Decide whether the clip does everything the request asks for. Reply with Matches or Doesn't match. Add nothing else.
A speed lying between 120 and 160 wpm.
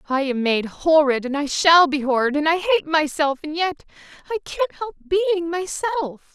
Doesn't match